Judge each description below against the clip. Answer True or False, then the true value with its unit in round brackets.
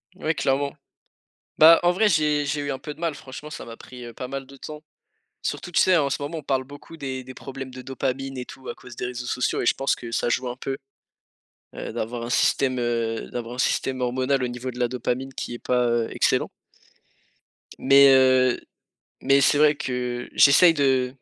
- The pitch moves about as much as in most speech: False (2.3 semitones)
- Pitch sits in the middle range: False (130 Hz)